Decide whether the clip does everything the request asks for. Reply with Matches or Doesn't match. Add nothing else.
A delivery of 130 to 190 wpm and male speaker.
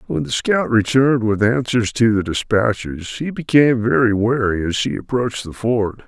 Matches